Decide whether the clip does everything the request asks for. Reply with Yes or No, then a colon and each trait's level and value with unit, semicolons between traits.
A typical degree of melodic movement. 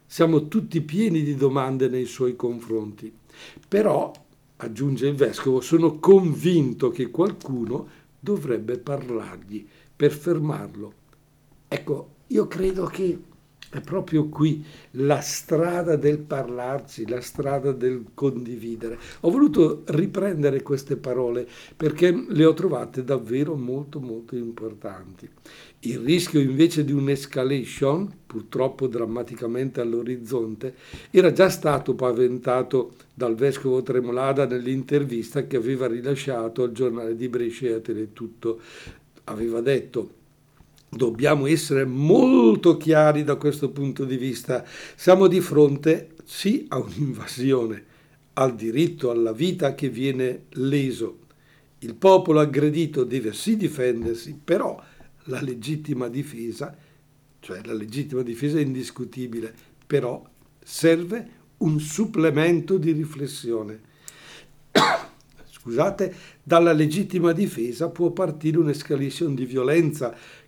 Yes: average, 4.2 semitones